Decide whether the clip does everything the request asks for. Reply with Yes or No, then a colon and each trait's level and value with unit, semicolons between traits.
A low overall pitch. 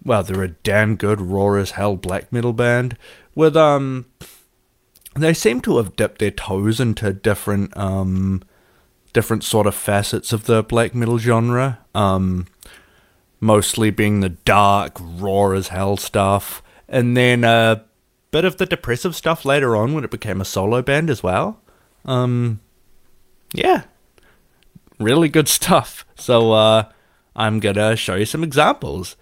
Yes: low, 110 Hz